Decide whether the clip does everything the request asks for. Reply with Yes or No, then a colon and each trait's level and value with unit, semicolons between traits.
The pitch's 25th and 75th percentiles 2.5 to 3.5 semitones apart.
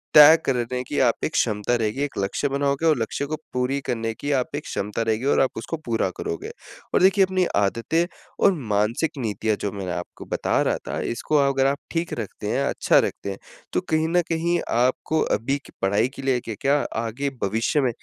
No: average, 4.9 semitones